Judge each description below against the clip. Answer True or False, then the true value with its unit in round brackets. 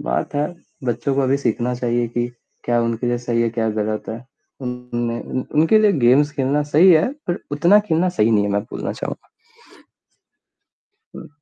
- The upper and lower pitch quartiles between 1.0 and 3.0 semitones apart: False (3.8 semitones)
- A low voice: True (125 Hz)